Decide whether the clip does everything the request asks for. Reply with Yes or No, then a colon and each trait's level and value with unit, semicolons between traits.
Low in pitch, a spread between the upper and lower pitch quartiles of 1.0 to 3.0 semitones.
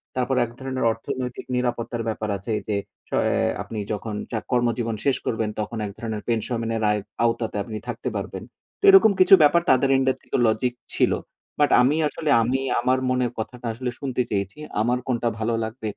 Yes: low, 120 Hz; narrow, 2.5 semitones